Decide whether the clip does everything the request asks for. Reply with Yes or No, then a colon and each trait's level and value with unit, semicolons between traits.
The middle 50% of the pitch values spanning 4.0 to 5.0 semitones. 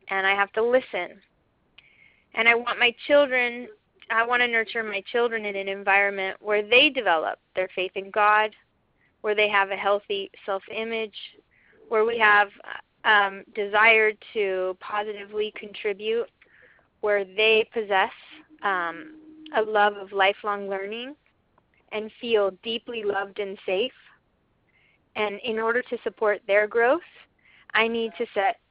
No: narrow, 2.6 semitones